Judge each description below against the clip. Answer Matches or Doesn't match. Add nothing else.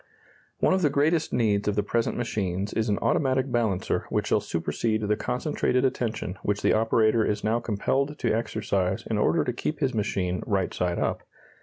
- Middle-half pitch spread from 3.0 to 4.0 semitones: Matches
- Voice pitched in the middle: Doesn't match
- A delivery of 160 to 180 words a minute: Doesn't match